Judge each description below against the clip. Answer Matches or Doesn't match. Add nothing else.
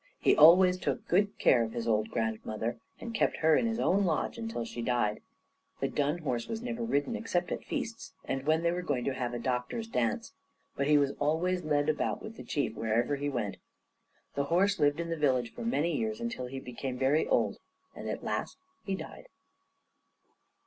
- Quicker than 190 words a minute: Matches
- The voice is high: Doesn't match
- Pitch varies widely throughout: Matches